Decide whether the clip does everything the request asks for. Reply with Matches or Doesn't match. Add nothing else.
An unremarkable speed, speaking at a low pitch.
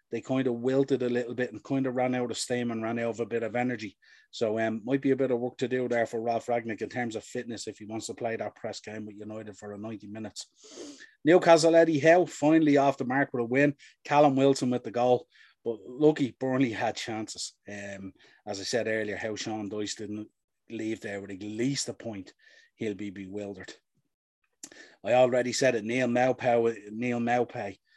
Doesn't match